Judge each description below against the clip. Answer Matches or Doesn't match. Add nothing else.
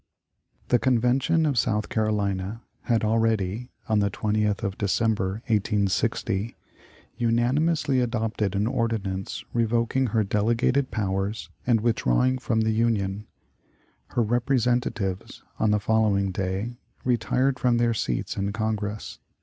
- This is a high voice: Doesn't match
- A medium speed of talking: Doesn't match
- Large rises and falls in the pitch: Doesn't match